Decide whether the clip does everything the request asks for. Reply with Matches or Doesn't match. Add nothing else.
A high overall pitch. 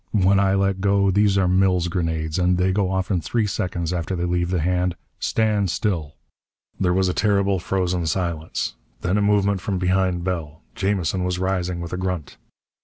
Doesn't match